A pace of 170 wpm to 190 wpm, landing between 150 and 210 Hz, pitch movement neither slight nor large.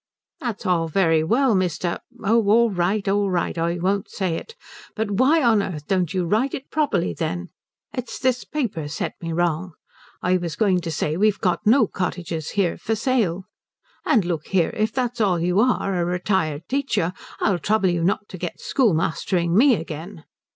Yes: average, 180 wpm; medium, 185 Hz; average, 4.4 semitones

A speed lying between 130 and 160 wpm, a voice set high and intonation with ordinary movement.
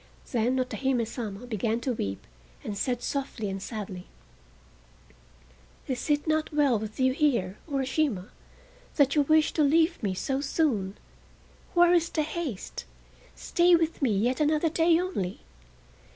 No: average, 140 wpm; very high, 265 Hz; wide, 6.1 semitones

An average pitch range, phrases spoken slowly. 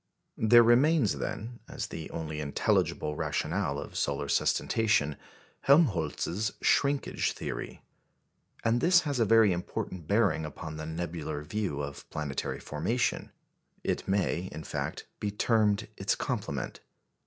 No: wide, 6.7 semitones; slow, 125 wpm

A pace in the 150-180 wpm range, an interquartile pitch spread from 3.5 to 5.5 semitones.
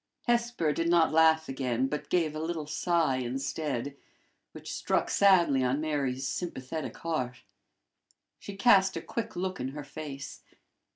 No: average, 140 wpm; average, 4.4 semitones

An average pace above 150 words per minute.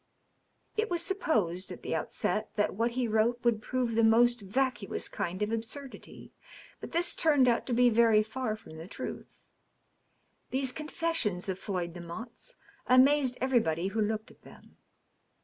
Yes: average, 160 wpm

